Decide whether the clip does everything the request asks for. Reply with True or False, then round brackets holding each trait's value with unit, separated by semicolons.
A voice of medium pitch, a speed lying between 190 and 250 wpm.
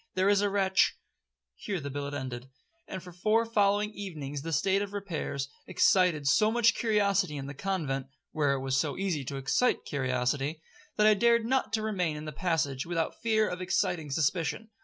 True (175 Hz; 195 wpm)